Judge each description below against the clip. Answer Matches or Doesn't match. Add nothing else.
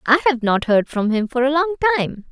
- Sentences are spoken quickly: Matches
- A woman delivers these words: Matches